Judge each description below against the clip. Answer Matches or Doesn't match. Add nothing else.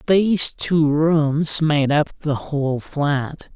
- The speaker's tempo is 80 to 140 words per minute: Matches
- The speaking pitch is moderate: Matches